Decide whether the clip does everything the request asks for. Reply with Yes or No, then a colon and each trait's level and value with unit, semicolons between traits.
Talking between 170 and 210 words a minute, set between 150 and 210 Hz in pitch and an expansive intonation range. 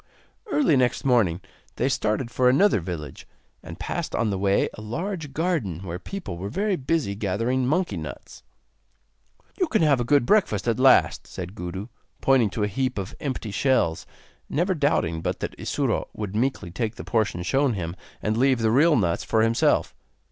No: average, 175 wpm; low, 115 Hz; wide, 6.1 semitones